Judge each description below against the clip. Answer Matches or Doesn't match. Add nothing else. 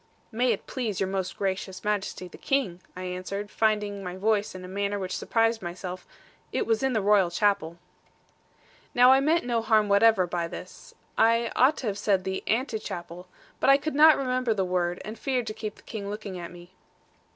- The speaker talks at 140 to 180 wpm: Doesn't match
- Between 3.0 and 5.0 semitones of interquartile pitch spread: Matches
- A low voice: Doesn't match